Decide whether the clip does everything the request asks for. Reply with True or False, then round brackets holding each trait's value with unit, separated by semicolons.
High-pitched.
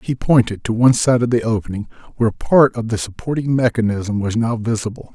False (115 Hz)